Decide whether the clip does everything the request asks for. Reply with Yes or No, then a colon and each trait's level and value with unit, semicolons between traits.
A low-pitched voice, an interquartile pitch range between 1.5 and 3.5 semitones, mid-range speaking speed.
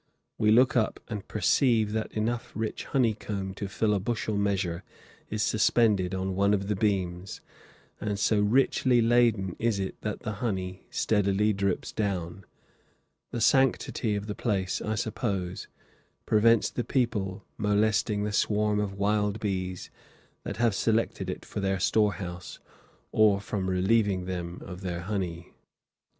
Yes: low, 105 Hz; narrow, 2.4 semitones; average, 145 wpm